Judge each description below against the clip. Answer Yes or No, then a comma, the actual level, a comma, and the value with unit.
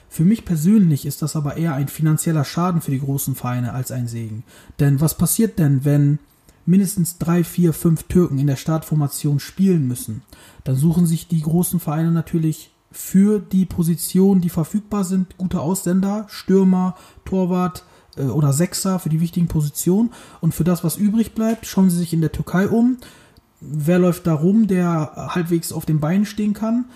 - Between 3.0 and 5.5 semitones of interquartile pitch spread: Yes, average, 3.7 semitones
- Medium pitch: Yes, medium, 170 Hz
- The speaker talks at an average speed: Yes, average, 175 wpm